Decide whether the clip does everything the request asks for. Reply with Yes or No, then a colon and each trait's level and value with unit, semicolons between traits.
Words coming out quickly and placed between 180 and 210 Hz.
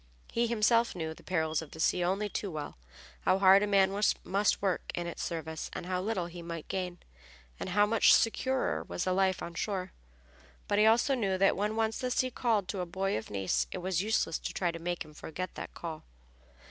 Yes: fast, 220 wpm; medium, 185 Hz